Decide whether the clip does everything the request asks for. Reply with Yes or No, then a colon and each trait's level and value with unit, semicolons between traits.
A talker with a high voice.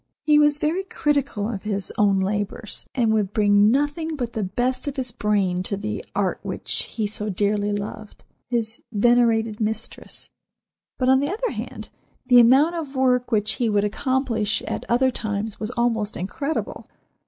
Yes: high, 225 Hz